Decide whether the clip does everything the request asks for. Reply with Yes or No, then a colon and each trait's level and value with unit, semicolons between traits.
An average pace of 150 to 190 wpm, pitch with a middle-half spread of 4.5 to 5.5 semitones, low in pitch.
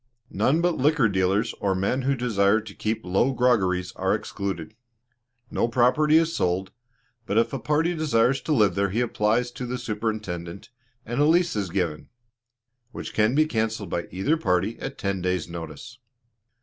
Yes: average, 170 wpm; average, 5.2 semitones; low, 110 Hz